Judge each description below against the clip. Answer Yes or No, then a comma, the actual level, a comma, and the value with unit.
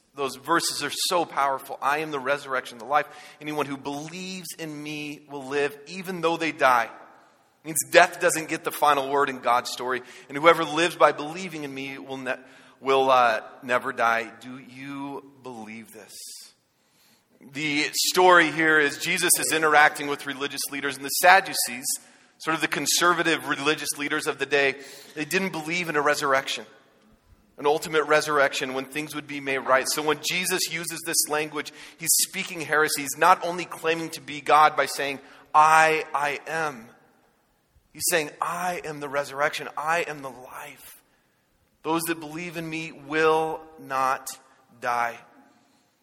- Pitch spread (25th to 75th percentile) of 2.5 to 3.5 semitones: Yes, average, 2.9 semitones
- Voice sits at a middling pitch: Yes, medium, 150 Hz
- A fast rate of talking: No, average, 165 wpm